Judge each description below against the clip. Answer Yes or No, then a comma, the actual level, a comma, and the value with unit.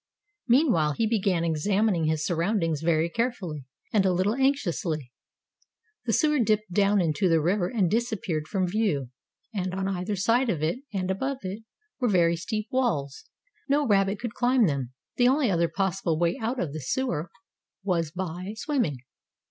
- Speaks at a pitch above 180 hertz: Yes, high, 190 Hz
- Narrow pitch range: No, average, 5.3 semitones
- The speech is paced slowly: No, average, 165 wpm